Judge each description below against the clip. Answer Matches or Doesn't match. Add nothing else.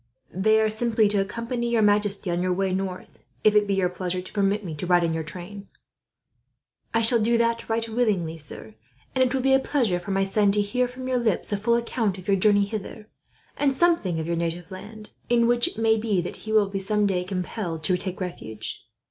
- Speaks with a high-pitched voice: Matches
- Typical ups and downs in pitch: Matches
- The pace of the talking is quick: Matches